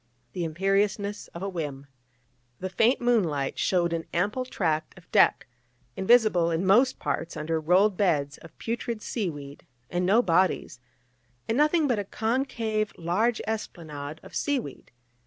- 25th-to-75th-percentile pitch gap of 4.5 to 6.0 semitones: Yes, average, 5.2 semitones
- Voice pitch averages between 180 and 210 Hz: Yes, high, 190 Hz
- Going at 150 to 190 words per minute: No, average, 140 wpm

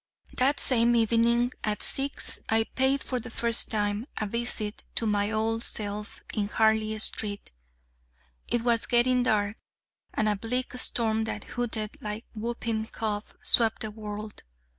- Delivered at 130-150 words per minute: Yes, average, 145 wpm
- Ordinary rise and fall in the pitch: No, narrow, 2.0 semitones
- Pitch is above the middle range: Yes, high, 225 Hz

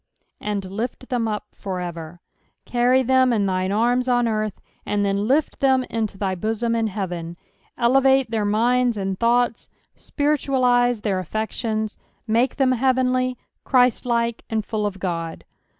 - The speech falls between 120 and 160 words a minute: Yes, average, 140 wpm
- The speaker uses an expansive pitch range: No, average, 3.7 semitones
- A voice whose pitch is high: Yes, high, 230 Hz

